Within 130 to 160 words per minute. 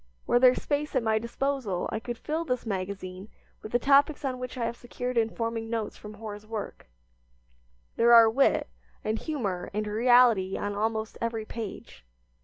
No: average, 170 wpm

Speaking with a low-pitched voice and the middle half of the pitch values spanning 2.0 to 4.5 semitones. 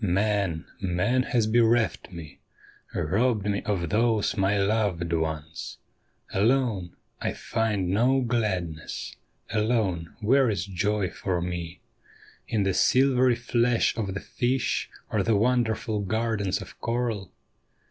Yes: low, 105 Hz; average, 4.1 semitones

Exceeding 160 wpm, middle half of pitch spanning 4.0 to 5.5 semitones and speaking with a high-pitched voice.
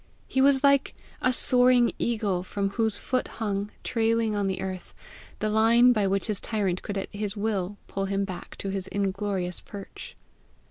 No: average, 175 wpm; average, 2.8 semitones; high, 205 Hz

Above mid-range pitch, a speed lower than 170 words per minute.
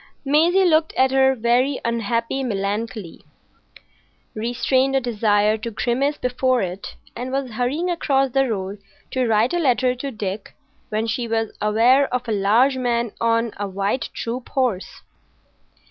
Yes: high, 240 Hz; average, 145 wpm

